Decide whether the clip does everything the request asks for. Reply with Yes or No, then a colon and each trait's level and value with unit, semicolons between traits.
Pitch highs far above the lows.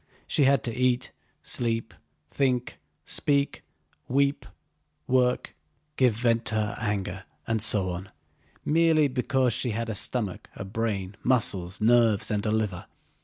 No: average, 3.5 semitones